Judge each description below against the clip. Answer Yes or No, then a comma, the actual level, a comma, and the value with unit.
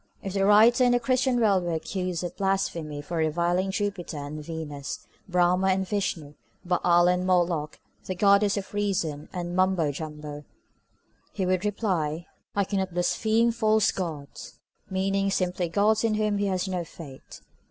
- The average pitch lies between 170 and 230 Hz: Yes, medium, 185 Hz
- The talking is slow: No, average, 155 wpm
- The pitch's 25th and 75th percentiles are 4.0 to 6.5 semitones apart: No, average, 3.3 semitones